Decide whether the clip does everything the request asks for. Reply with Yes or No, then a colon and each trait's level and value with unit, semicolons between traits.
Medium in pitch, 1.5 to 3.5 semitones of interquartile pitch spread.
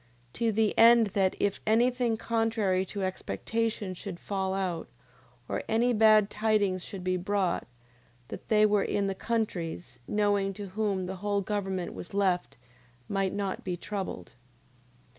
No: high, 200 Hz; narrow, 2.6 semitones